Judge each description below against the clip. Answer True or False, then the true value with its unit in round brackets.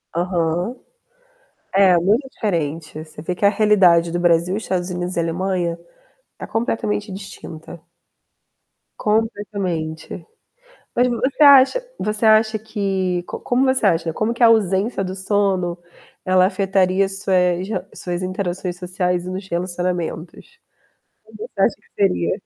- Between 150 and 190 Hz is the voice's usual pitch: True (185 Hz)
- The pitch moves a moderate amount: True (3.2 semitones)